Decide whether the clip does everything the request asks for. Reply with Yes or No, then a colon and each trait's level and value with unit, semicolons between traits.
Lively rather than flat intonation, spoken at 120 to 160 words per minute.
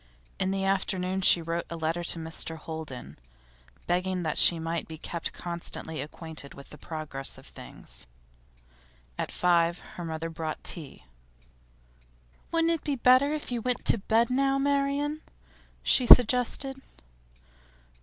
Yes: wide, 7.6 semitones; average, 140 wpm